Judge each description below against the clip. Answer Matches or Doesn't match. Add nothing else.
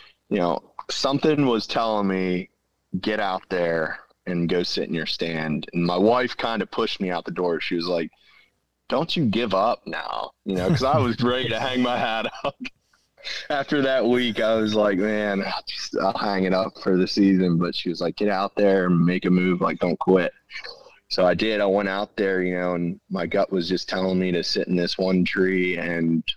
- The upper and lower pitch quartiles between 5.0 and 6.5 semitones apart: Doesn't match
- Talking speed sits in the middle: Doesn't match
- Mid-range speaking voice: Doesn't match